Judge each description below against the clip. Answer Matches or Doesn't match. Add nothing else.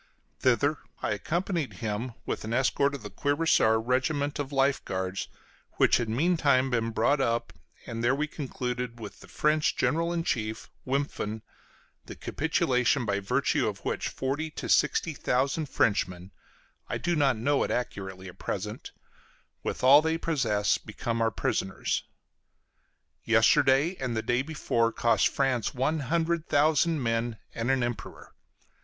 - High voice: Doesn't match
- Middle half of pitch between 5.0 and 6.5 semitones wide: Doesn't match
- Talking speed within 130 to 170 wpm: Matches